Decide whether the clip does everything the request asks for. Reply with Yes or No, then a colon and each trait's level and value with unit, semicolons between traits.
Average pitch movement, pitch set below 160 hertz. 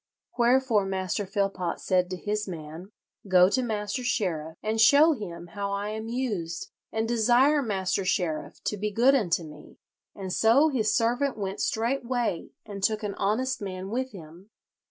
No: average, 4.4 semitones; high, 210 Hz